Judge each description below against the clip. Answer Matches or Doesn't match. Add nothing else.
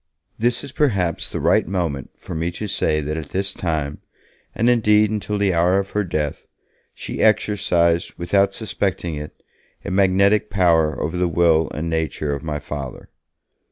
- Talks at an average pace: Matches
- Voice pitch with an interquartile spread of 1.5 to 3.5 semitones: Doesn't match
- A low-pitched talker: Matches